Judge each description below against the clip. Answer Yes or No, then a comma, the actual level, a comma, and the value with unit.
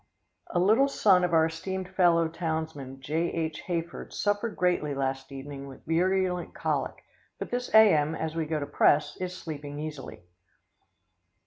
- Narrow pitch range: No, average, 3.7 semitones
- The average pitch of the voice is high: No, medium, 165 Hz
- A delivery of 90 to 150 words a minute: Yes, average, 145 wpm